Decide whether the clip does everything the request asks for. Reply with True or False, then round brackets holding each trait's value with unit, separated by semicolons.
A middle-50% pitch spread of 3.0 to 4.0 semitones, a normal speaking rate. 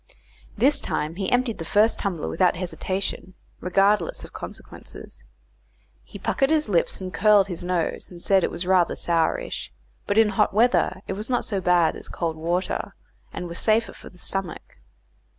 True (3.4 semitones; 170 wpm)